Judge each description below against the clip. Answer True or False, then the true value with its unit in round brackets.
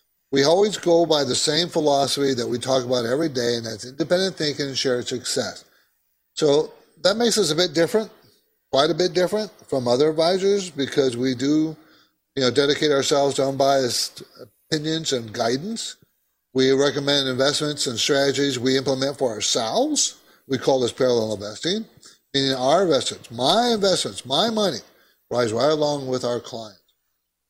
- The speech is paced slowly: False (160 wpm)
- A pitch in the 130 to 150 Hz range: True (140 Hz)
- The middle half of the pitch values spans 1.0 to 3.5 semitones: False (4.4 semitones)